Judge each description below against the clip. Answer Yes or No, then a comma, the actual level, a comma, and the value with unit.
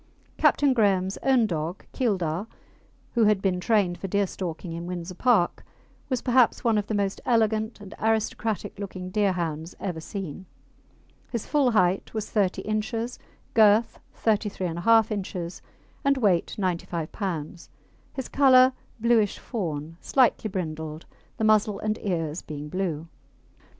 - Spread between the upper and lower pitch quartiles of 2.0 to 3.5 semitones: No, average, 4.2 semitones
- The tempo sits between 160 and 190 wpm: No, slow, 135 wpm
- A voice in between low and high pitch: No, high, 200 Hz